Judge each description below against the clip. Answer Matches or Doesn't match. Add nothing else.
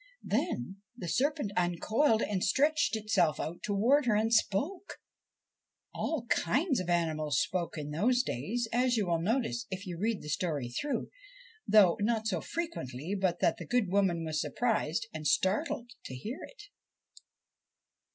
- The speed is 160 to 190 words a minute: Doesn't match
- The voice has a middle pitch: Doesn't match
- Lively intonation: Matches